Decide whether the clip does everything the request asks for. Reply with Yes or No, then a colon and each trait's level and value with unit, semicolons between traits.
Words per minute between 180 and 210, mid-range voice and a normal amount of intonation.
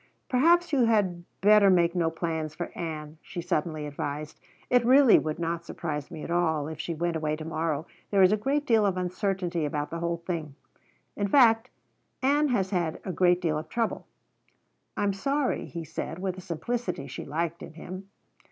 Yes: average, 190 wpm; medium, 175 Hz; average, 4.5 semitones